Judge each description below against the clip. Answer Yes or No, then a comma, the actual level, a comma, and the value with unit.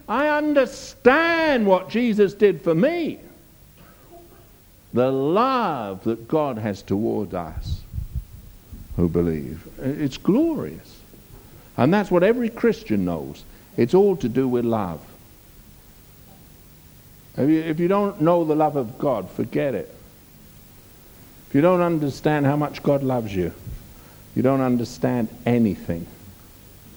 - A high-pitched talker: No, low, 125 Hz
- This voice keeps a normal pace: No, slow, 120 wpm